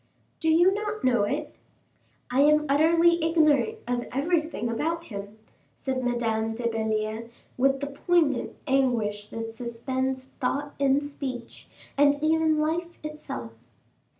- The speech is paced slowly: Yes, slow, 125 wpm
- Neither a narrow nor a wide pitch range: Yes, average, 5.0 semitones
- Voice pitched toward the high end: Yes, very high, 275 Hz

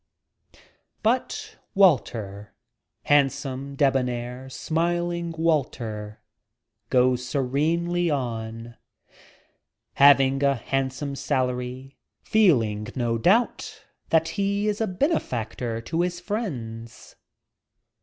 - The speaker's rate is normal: No, slow, 85 wpm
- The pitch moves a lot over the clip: Yes, wide, 5.9 semitones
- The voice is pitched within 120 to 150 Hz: Yes, low, 135 Hz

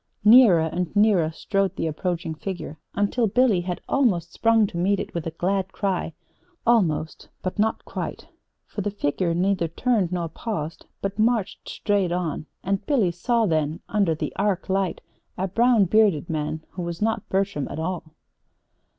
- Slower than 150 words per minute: No, average, 165 wpm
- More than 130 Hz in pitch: Yes, high, 190 Hz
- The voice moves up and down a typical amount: Yes, average, 3.9 semitones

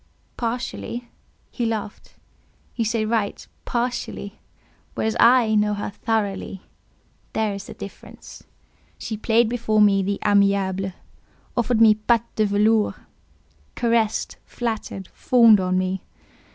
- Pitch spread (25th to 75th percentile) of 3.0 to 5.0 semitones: No, narrow, 2.5 semitones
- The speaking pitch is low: No, high, 215 Hz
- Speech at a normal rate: No, slow, 110 wpm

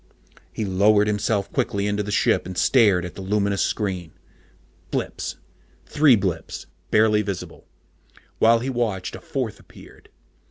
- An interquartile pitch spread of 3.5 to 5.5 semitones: No, narrow, 2.4 semitones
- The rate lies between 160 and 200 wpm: No, average, 145 wpm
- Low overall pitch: Yes, low, 105 Hz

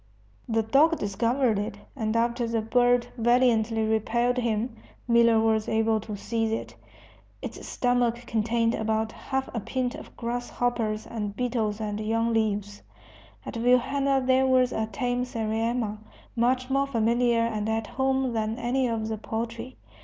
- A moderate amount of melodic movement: No, narrow, 2.0 semitones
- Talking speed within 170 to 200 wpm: No, average, 150 wpm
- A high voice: Yes, high, 230 Hz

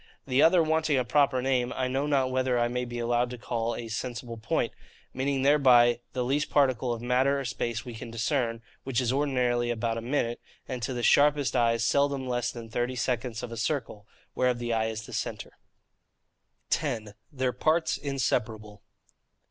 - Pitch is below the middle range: Yes, low, 125 Hz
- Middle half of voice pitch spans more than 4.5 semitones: No, narrow, 2.4 semitones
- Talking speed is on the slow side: No, average, 185 wpm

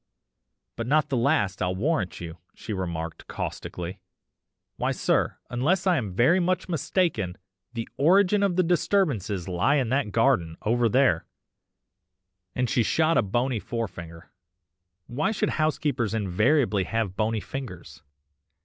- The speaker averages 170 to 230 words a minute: No, slow, 135 wpm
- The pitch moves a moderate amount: No, wide, 7.9 semitones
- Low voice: Yes, low, 115 Hz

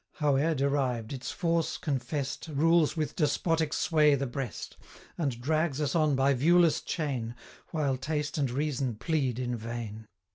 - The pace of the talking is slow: No, average, 150 wpm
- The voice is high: No, medium, 140 Hz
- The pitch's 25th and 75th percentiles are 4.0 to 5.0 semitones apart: No, average, 3.6 semitones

